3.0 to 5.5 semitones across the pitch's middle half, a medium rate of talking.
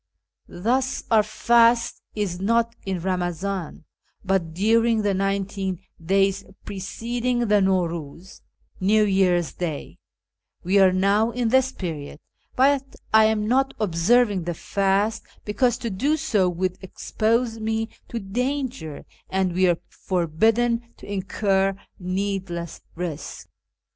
No: average, 3.8 semitones; slow, 125 wpm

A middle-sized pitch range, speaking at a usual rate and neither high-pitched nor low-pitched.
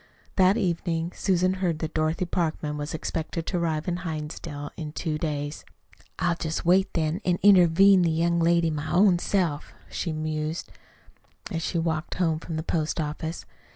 No: narrow, 2.1 semitones; average, 165 wpm; medium, 165 Hz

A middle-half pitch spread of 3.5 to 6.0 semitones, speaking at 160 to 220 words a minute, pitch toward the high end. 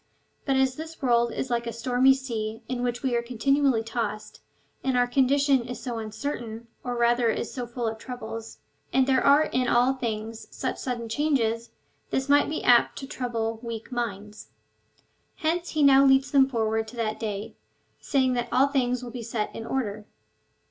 No: average, 2.8 semitones; average, 185 wpm; high, 245 Hz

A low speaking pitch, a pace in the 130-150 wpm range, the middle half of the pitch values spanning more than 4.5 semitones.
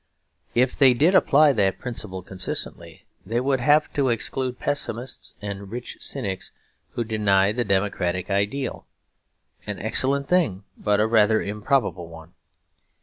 Yes: low, 110 Hz; slow, 135 wpm; average, 5.2 semitones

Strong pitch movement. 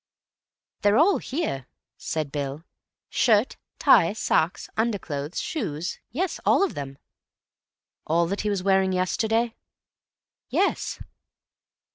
Yes: wide, 6.6 semitones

